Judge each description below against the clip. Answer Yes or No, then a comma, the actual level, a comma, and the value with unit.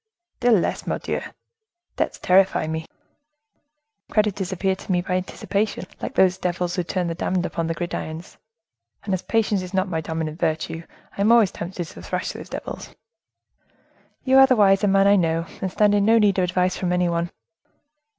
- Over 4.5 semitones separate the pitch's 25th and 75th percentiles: No, average, 2.7 semitones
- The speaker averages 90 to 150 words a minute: No, average, 180 wpm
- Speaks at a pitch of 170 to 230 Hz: Yes, medium, 185 Hz